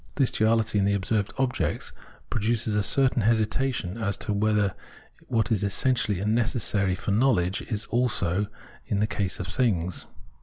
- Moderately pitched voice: No, low, 105 Hz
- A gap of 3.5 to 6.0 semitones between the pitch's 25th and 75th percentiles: No, average, 2.9 semitones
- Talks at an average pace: Yes, average, 160 wpm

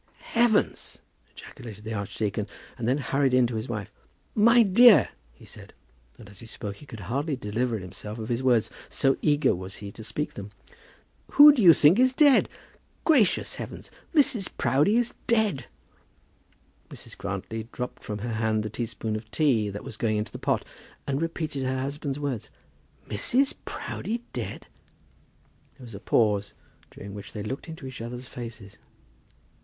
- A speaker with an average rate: Yes, average, 170 wpm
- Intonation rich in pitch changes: Yes, wide, 6.3 semitones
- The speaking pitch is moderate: No, low, 125 Hz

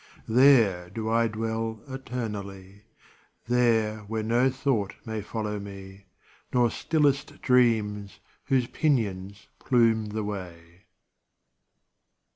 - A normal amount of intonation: Yes, average, 3.2 semitones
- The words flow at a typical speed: No, slow, 95 wpm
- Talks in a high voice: No, low, 110 Hz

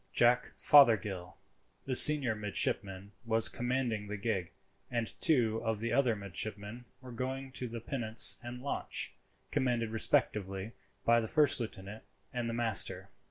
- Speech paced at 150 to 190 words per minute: No, average, 140 wpm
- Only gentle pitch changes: No, average, 3.0 semitones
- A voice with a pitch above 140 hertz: No, low, 115 Hz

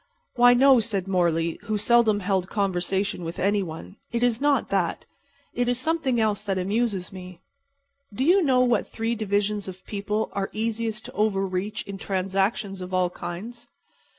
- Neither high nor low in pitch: No, high, 205 Hz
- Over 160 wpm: Yes, average, 170 wpm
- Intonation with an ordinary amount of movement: Yes, average, 3.7 semitones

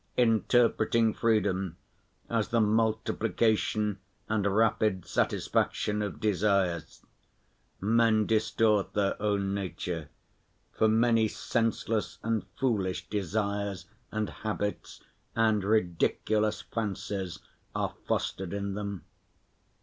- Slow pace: Yes, slow, 90 wpm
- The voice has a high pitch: No, low, 105 Hz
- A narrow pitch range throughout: Yes, narrow, 2.0 semitones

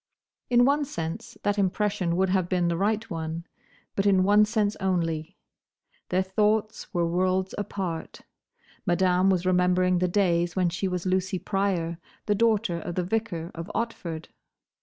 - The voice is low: No, medium, 185 Hz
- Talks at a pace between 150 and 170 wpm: Yes, average, 155 wpm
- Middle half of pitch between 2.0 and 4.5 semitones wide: Yes, average, 2.9 semitones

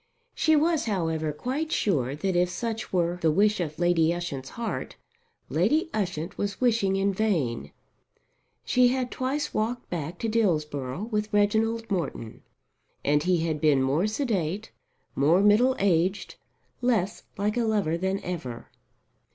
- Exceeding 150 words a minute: No, average, 145 wpm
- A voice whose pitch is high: Yes, high, 195 Hz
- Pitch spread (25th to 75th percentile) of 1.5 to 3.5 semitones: No, wide, 5.5 semitones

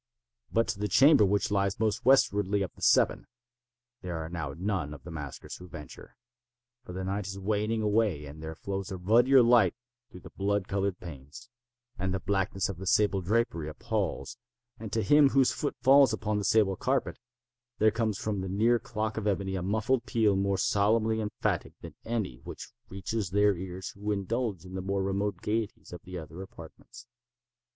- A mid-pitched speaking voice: No, low, 100 Hz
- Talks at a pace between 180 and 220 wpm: Yes, average, 185 wpm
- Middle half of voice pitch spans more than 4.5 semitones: No, average, 3.1 semitones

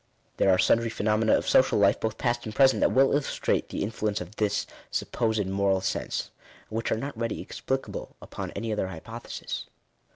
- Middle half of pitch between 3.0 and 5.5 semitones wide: No, narrow, 2.4 semitones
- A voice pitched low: Yes, low, 110 Hz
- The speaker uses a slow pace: No, average, 190 wpm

